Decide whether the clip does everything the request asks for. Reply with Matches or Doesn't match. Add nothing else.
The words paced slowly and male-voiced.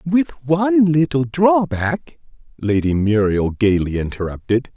Matches